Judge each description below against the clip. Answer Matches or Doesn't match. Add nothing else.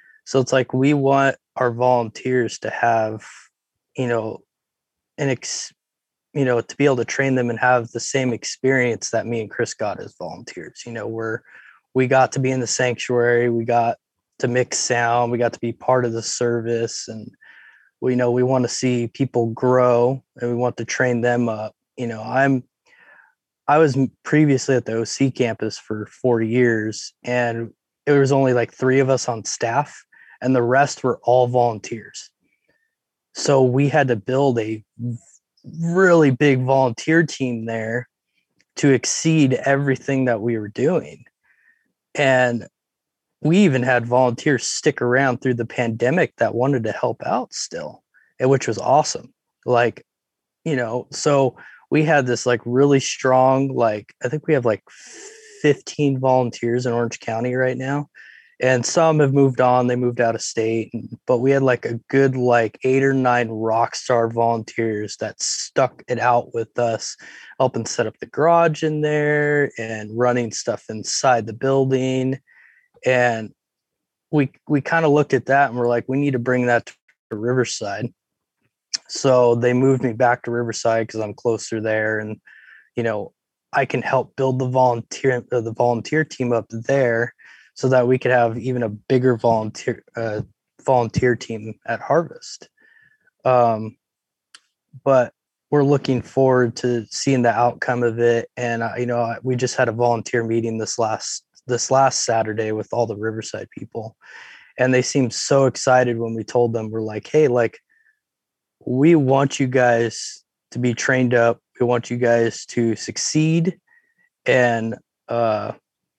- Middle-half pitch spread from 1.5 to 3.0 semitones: Matches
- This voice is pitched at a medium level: Doesn't match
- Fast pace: Doesn't match